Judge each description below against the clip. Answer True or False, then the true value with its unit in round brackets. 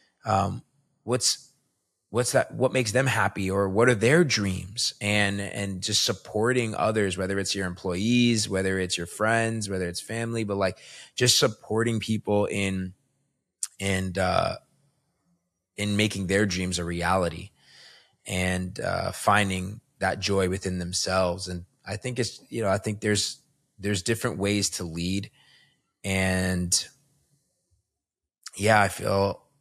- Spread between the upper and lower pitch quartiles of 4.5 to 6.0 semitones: False (3.4 semitones)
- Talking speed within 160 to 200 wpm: False (140 wpm)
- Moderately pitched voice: False (100 Hz)